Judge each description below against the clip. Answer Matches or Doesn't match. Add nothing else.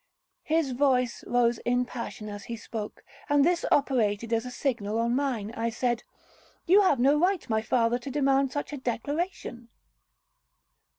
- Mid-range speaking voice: Doesn't match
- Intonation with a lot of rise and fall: Doesn't match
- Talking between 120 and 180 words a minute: Matches